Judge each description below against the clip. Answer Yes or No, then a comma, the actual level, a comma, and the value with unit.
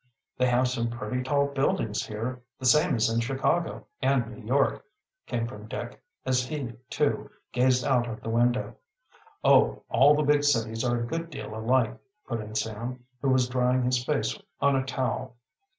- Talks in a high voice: No, low, 125 Hz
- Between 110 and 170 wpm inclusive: No, average, 180 wpm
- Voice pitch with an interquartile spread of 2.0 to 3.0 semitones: Yes, narrow, 2.4 semitones